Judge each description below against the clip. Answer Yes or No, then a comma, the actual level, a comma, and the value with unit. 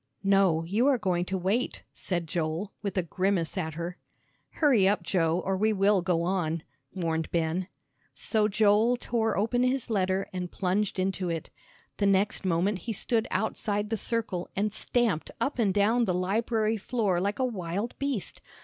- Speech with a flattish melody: No, average, 3.4 semitones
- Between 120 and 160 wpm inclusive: No, average, 170 wpm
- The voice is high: Yes, high, 195 Hz